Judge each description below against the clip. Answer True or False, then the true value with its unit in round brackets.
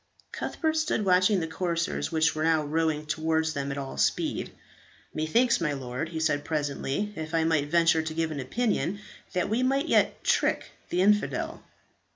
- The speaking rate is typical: True (175 wpm)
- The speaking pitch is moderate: True (160 Hz)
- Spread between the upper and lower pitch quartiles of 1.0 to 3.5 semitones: True (3.2 semitones)